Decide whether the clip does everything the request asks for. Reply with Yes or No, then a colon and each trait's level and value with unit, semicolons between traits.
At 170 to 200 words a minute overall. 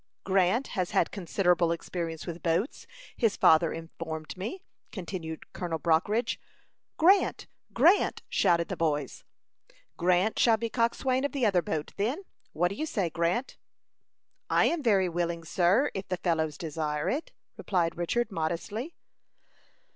No: average, 140 wpm